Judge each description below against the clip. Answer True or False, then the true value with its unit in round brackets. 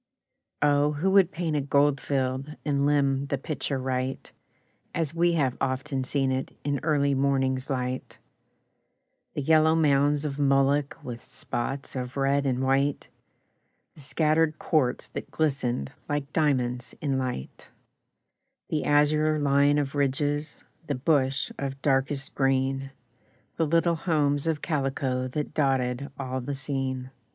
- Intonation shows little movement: True (1.9 semitones)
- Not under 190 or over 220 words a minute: False (135 wpm)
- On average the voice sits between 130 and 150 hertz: True (140 Hz)